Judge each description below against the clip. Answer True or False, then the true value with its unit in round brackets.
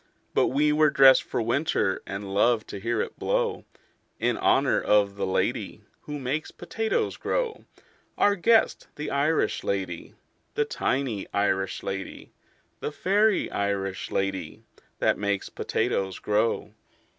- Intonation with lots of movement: True (7.3 semitones)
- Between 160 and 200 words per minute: False (135 wpm)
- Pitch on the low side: True (110 Hz)